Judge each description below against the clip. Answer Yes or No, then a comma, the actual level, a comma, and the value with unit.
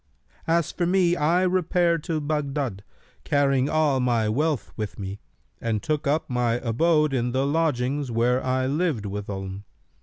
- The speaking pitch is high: No, medium, 140 Hz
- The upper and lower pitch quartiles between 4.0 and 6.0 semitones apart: Yes, average, 5.0 semitones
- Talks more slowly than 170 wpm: Yes, average, 150 wpm